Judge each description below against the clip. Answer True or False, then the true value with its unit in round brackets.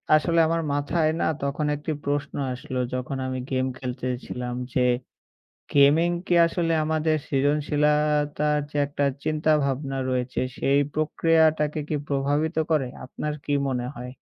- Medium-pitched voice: True (145 Hz)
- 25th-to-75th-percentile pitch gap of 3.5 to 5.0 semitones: False (2.5 semitones)